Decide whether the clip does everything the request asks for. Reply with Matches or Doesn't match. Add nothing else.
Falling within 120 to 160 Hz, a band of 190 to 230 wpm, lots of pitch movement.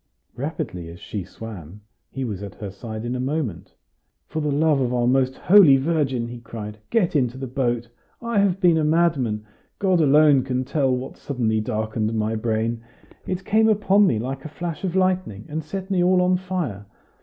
Matches